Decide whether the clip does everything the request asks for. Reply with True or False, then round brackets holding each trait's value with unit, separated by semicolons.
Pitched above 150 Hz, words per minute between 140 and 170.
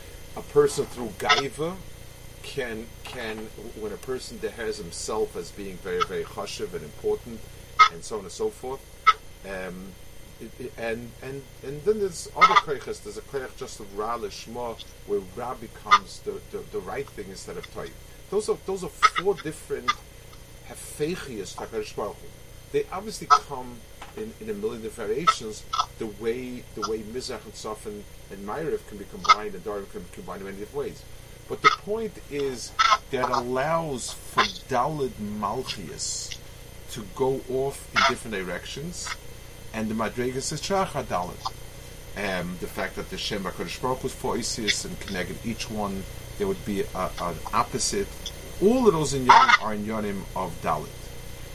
False (140 Hz; 160 wpm)